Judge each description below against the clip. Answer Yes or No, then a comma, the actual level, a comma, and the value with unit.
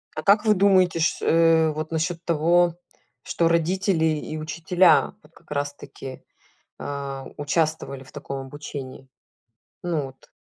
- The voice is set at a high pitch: No, medium, 160 Hz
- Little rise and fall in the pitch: No, average, 3.0 semitones